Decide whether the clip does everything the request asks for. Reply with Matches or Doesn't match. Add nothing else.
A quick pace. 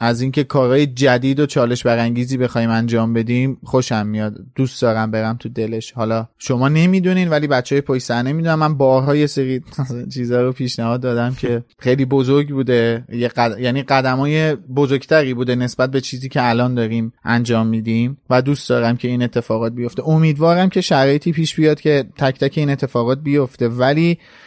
Matches